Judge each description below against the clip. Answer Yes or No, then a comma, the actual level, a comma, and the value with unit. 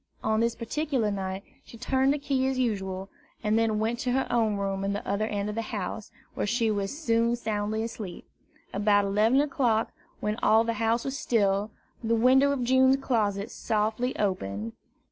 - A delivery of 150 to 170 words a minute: No, average, 185 wpm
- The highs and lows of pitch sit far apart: No, average, 3.3 semitones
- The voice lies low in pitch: No, high, 220 Hz